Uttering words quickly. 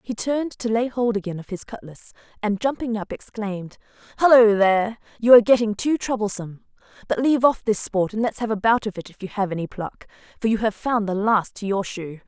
Yes: fast, 225 wpm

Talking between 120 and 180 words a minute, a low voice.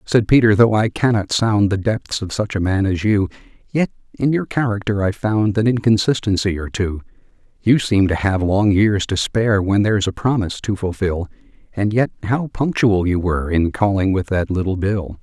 No: average, 195 wpm; low, 100 Hz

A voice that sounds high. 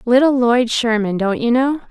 Yes: high, 240 Hz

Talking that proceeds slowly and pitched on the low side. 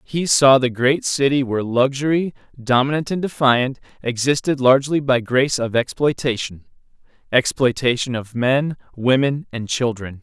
Yes: slow, 130 wpm; low, 130 Hz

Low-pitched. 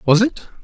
No: medium, 185 Hz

